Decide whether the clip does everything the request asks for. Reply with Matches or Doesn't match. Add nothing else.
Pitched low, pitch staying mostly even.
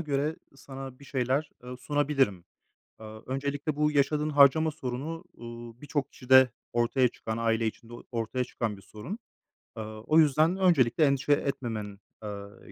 Doesn't match